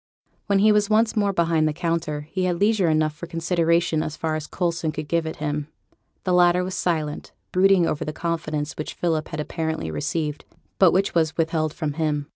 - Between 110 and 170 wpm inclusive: No, average, 200 wpm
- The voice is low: No, medium, 165 Hz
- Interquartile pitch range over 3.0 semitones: No, narrow, 2.6 semitones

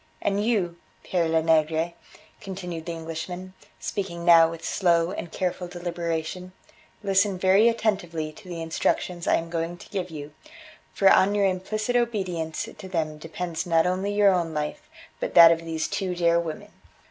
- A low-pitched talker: No, medium, 175 Hz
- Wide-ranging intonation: No, narrow, 2.6 semitones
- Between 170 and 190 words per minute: No, average, 160 wpm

